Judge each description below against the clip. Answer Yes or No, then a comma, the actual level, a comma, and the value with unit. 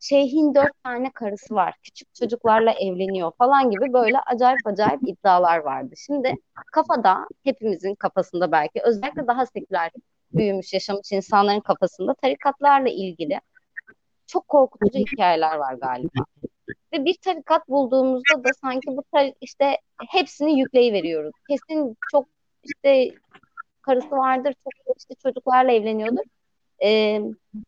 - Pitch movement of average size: No, wide, 5.9 semitones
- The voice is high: Yes, very high, 250 Hz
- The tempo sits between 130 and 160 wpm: No, average, 120 wpm